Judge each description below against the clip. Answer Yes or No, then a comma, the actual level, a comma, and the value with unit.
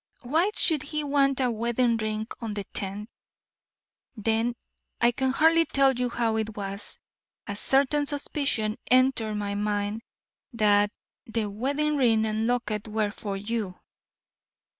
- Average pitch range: Yes, average, 4.1 semitones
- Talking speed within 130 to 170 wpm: Yes, average, 140 wpm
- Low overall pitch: No, high, 230 Hz